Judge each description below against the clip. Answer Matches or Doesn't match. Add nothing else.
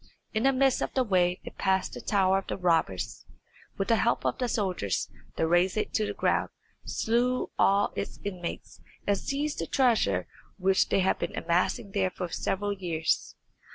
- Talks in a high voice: Matches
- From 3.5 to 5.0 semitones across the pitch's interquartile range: Matches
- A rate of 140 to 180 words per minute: Doesn't match